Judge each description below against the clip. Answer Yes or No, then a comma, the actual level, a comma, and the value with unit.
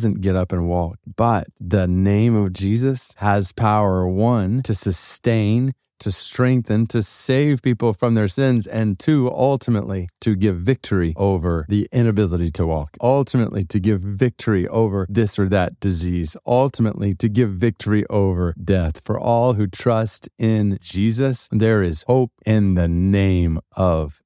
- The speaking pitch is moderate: No, low, 105 Hz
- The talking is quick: No, average, 150 wpm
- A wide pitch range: No, average, 3.7 semitones